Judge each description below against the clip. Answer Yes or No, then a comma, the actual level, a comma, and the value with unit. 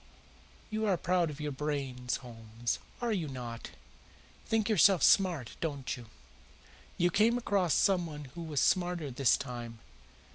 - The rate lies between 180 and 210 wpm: No, average, 140 wpm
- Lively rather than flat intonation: Yes, wide, 6.5 semitones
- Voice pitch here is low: No, medium, 150 Hz